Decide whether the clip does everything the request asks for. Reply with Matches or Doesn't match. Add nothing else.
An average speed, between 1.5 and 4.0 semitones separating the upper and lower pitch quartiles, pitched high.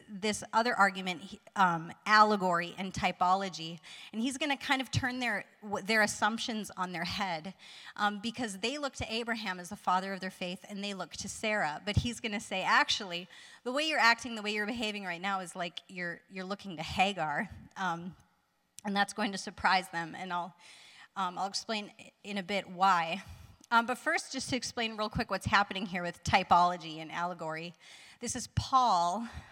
Matches